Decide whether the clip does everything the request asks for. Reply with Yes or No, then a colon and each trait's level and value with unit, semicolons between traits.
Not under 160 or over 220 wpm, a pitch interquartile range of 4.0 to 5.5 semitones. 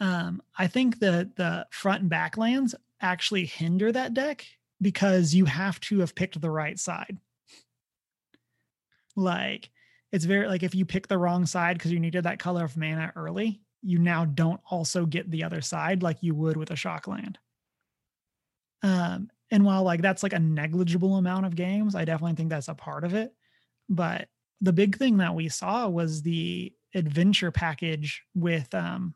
No: average, 180 wpm; average, 2.8 semitones